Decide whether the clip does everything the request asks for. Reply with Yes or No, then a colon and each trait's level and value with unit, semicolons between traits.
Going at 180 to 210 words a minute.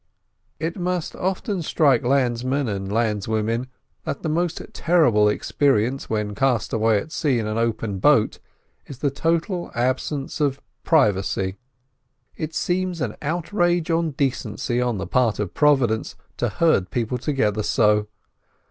No: average, 140 wpm